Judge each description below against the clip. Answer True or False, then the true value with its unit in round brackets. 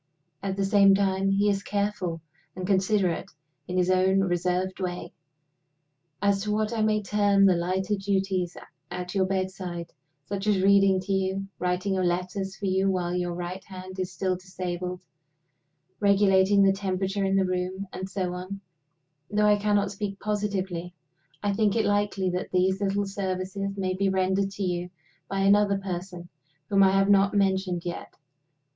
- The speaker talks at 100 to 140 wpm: False (165 wpm)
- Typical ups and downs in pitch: False (1.4 semitones)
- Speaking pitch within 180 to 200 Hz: True (190 Hz)